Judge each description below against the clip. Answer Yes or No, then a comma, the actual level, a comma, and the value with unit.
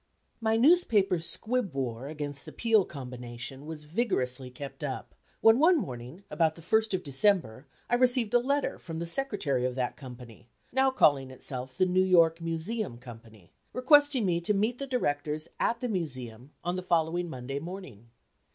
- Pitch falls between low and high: Yes, medium, 165 Hz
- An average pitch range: No, wide, 9.0 semitones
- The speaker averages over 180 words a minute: No, average, 170 wpm